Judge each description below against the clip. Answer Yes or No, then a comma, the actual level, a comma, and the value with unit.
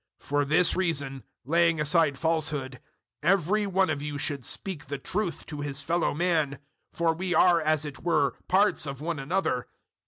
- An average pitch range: Yes, average, 3.5 semitones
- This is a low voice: No, medium, 155 Hz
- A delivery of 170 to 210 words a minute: Yes, average, 175 wpm